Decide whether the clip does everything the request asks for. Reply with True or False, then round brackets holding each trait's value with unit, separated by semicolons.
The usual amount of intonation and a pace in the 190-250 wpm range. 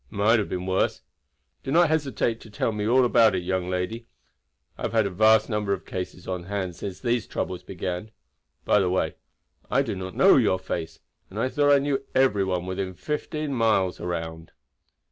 True (4.2 semitones; 200 wpm)